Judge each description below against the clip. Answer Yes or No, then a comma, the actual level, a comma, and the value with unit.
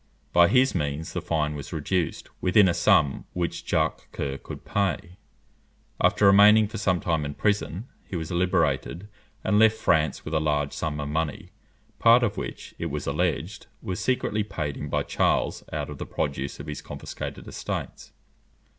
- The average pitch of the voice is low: Yes, very low, 85 Hz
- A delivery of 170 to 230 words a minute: Yes, average, 175 wpm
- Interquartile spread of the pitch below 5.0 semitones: No, average, 5.3 semitones